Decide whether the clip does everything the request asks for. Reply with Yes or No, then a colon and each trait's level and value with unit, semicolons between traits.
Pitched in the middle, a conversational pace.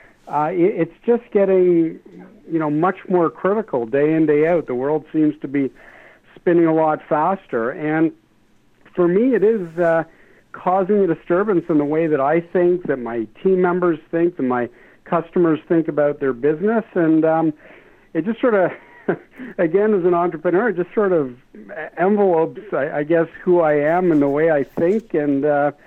Yes: medium, 165 Hz; average, 175 wpm